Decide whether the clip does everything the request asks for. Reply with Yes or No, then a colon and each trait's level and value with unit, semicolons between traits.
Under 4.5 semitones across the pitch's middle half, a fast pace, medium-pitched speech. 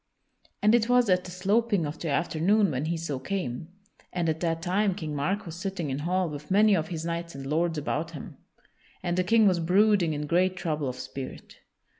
Yes: average, 3.8 semitones; fast, 210 wpm; medium, 170 Hz